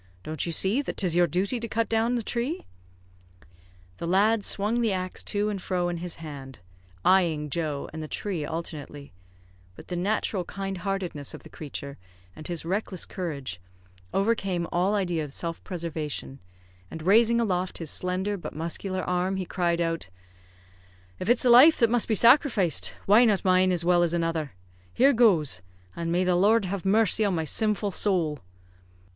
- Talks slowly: No, average, 175 wpm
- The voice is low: No, medium, 185 Hz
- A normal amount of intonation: Yes, average, 3.9 semitones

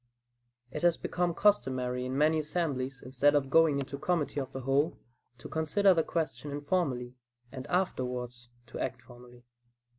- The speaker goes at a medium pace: Yes, average, 150 wpm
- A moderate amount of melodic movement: Yes, average, 4.3 semitones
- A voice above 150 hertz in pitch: No, medium, 140 Hz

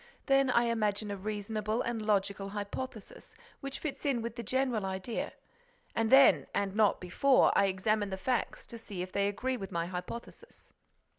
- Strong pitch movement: No, average, 3.2 semitones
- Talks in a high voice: Yes, high, 215 Hz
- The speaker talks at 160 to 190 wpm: Yes, average, 170 wpm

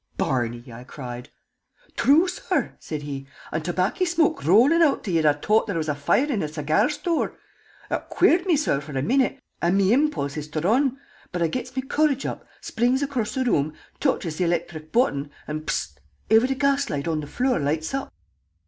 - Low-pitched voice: No, medium, 185 Hz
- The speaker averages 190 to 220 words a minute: Yes, average, 195 wpm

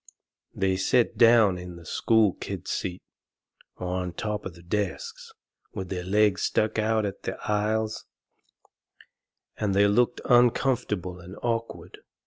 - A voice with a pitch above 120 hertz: No, low, 105 Hz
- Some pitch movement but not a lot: Yes, average, 3.4 semitones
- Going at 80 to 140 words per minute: Yes, slow, 135 wpm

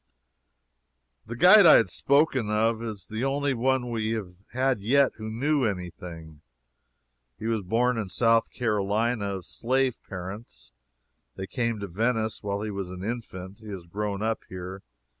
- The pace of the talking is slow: No, average, 160 wpm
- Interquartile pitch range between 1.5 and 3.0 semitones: No, average, 3.8 semitones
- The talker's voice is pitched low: Yes, low, 110 Hz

